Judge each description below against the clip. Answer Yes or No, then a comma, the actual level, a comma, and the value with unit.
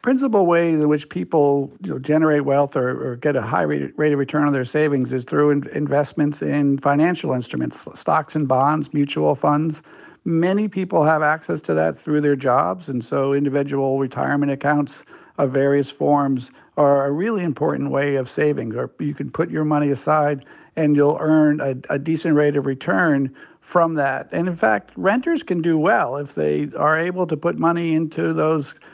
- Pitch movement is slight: Yes, narrow, 2.1 semitones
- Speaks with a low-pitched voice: No, medium, 145 Hz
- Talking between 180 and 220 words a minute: Yes, average, 185 wpm